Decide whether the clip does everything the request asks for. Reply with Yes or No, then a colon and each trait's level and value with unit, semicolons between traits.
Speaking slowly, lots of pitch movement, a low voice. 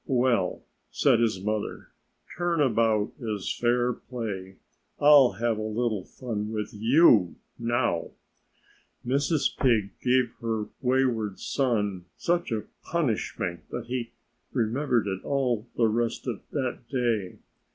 No: slow, 120 wpm; average, 3.2 semitones; low, 115 Hz